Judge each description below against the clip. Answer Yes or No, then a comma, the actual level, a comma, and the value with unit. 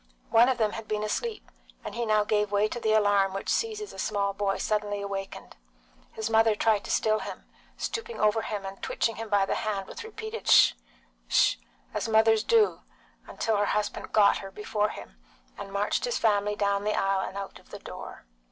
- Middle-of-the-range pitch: No, high, 210 Hz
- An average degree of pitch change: No, narrow, 1.9 semitones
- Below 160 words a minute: No, average, 200 wpm